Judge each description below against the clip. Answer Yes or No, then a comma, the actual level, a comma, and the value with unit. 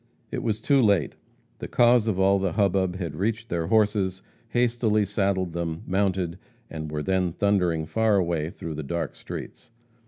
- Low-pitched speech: Yes, very low, 95 Hz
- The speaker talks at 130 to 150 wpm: No, average, 165 wpm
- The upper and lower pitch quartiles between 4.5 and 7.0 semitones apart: No, average, 3.8 semitones